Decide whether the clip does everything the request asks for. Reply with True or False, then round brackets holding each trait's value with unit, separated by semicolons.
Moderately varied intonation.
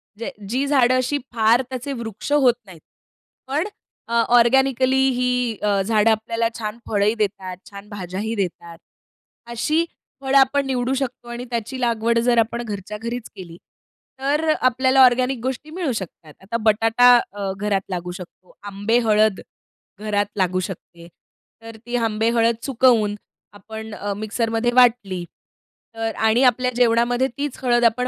True (3.3 semitones)